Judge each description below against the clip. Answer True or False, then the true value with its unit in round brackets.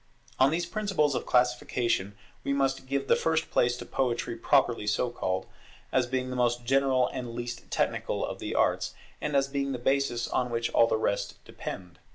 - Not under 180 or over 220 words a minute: True (195 wpm)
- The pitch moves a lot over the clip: False (2.5 semitones)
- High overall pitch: False (125 Hz)